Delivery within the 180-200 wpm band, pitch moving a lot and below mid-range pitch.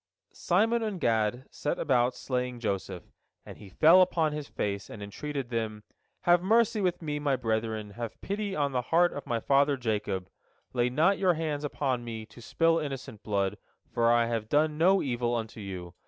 Yes: average, 185 wpm; wide, 6.2 semitones; low, 130 Hz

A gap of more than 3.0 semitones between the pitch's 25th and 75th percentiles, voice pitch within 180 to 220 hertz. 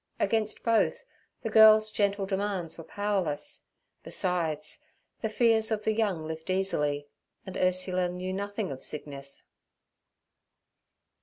Yes: average, 4.6 semitones; high, 190 Hz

